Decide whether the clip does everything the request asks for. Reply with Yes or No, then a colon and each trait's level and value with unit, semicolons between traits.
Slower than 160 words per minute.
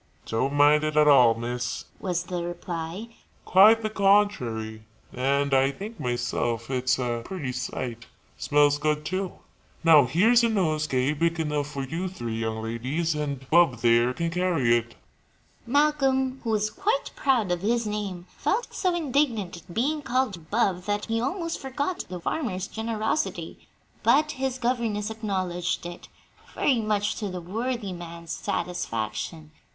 Yes: average, 150 wpm